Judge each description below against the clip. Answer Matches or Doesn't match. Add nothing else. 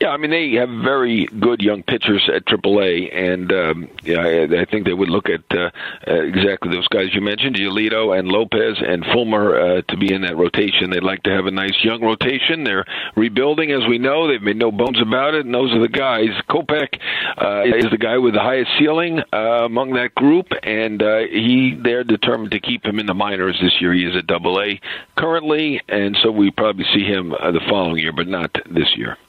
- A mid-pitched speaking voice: Doesn't match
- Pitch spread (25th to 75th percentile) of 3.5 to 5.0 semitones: Matches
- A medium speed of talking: Doesn't match